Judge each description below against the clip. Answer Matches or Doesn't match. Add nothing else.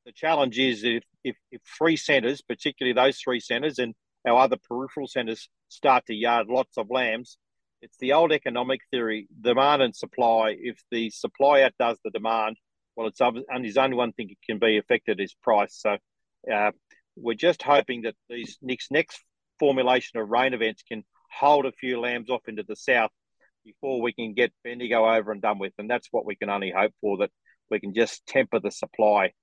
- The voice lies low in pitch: Matches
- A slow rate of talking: Doesn't match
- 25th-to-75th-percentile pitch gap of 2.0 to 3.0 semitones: Matches